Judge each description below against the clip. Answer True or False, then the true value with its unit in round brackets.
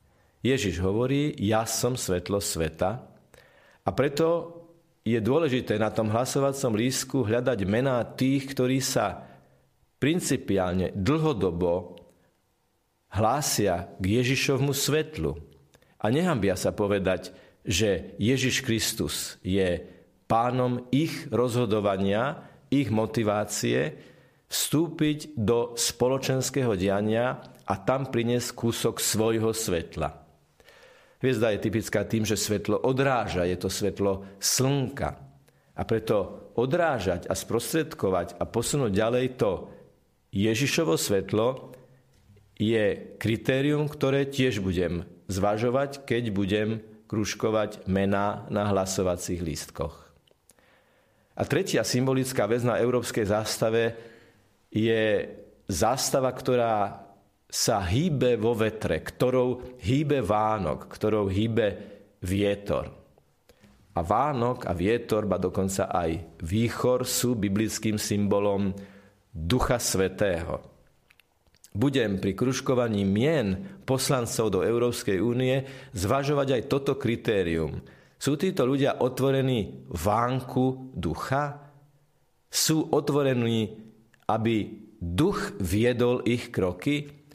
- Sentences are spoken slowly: True (95 wpm)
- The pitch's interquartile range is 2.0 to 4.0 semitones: False (4.6 semitones)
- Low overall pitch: True (115 Hz)